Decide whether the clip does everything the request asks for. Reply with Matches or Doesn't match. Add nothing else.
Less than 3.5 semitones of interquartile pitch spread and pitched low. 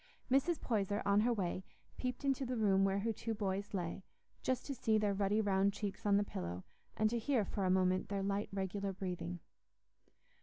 Doesn't match